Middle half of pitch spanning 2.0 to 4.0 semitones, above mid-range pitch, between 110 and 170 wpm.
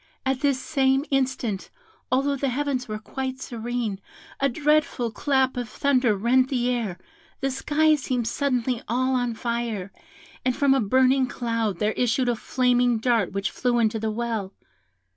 Yes: narrow, 2.6 semitones; very high, 250 Hz; average, 160 wpm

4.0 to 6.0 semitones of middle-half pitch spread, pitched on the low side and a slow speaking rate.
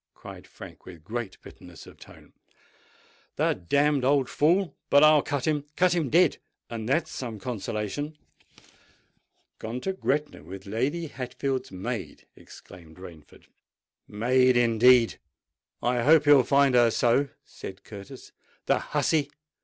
Yes: average, 5.0 semitones; low, 130 Hz; slow, 120 wpm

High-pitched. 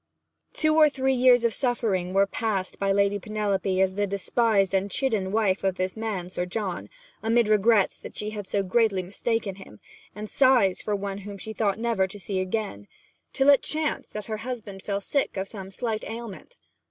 Yes: high, 205 Hz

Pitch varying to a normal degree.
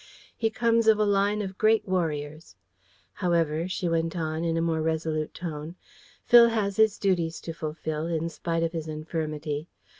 Yes: average, 3.9 semitones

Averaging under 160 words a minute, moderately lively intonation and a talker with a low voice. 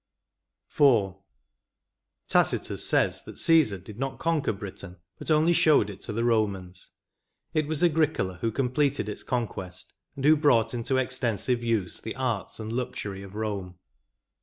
No: average, 145 wpm; wide, 5.7 semitones; low, 115 Hz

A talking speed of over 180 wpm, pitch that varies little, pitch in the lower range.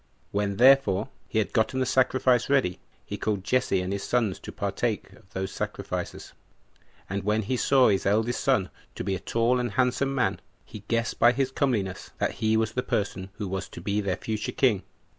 No: average, 200 wpm; average, 4.2 semitones; low, 110 Hz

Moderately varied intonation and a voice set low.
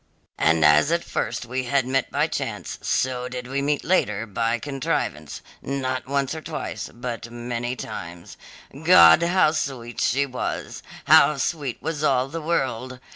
Yes: average, 3.1 semitones; low, 130 Hz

